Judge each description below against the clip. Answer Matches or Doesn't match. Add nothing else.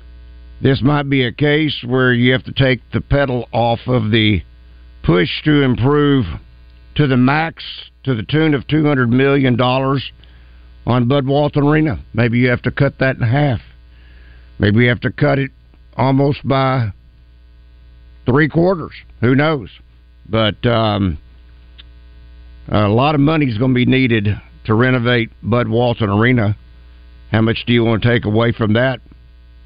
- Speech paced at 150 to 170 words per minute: Matches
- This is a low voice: Matches